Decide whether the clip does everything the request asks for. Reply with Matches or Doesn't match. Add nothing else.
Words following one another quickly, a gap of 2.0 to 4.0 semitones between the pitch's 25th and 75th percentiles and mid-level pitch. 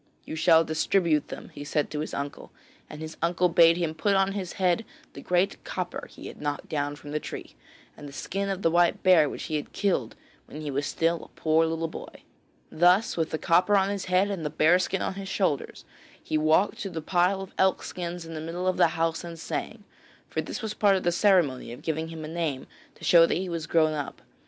Matches